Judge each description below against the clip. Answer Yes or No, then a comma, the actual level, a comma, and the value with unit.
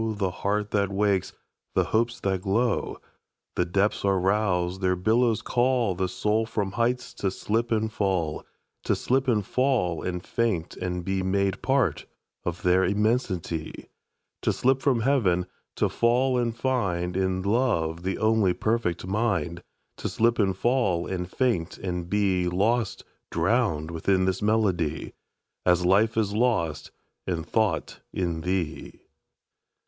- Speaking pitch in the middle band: No, low, 100 Hz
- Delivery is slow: Yes, slow, 125 wpm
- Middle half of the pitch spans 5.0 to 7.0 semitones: No, average, 4.2 semitones